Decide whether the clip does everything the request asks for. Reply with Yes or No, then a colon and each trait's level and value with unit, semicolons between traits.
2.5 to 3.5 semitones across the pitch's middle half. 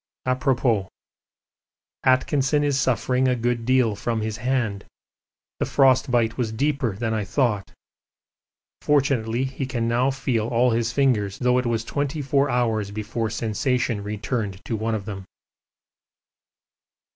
Yes: average, 3.0 semitones